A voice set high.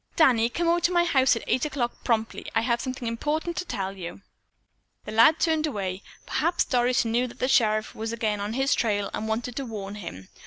Yes: high, 235 Hz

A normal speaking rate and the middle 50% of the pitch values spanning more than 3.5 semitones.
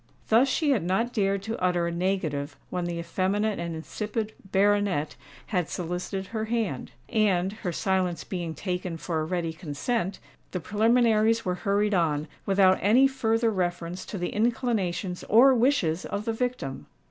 Yes: average, 160 wpm; average, 4.1 semitones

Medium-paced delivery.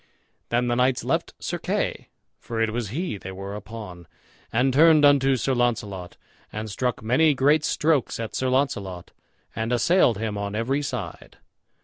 Yes: average, 160 wpm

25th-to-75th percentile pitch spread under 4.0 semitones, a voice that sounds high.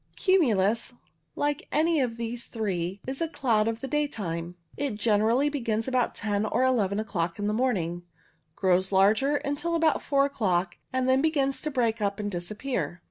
No: wide, 5.4 semitones; high, 230 Hz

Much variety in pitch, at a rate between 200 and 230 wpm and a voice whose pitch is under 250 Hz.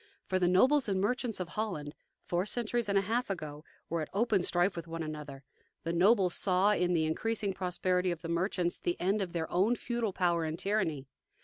No: average, 3.6 semitones; fast, 205 wpm; medium, 185 Hz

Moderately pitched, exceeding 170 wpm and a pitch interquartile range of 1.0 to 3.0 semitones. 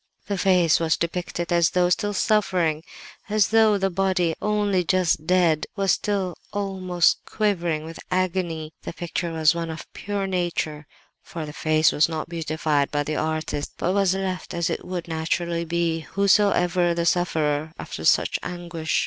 No: medium, 175 Hz; average, 160 wpm; narrow, 2.6 semitones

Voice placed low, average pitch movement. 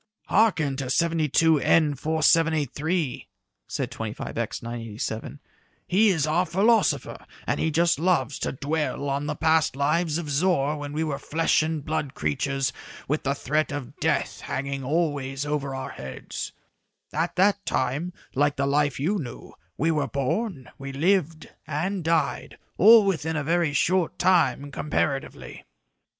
No: medium, 150 Hz; average, 3.2 semitones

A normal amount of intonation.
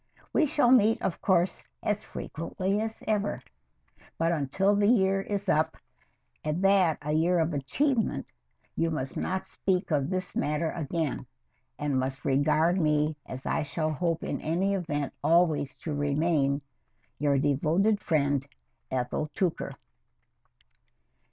Yes: average, 4.7 semitones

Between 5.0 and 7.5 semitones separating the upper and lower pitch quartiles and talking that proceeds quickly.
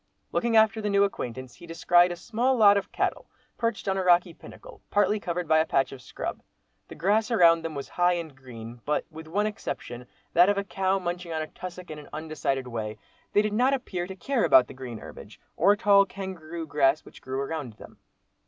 Yes: wide, 5.4 semitones; fast, 210 wpm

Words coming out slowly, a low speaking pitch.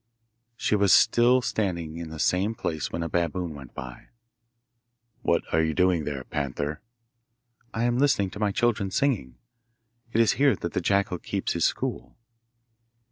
No: average, 160 wpm; very low, 90 Hz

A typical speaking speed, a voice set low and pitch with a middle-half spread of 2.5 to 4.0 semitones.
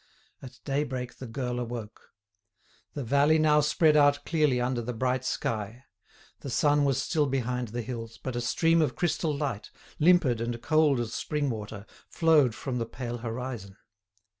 Yes: average, 165 wpm; low, 130 Hz; average, 3.7 semitones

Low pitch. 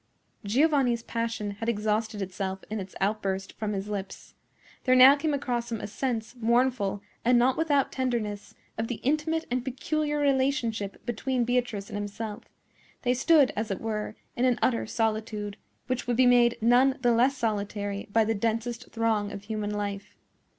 No: high, 230 Hz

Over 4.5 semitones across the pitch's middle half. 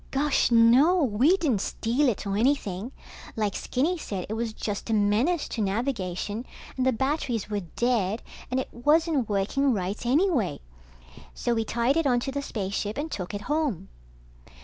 Yes: average, 5.2 semitones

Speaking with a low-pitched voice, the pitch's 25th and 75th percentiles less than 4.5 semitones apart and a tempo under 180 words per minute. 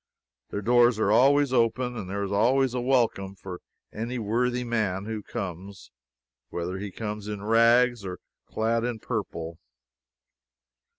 Yes: low, 110 Hz; average, 3.6 semitones; average, 140 wpm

